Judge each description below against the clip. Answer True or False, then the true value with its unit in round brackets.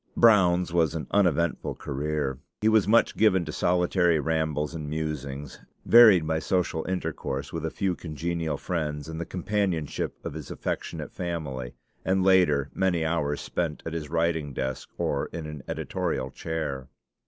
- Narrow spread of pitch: False (3.0 semitones)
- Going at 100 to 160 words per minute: True (155 wpm)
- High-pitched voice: False (80 Hz)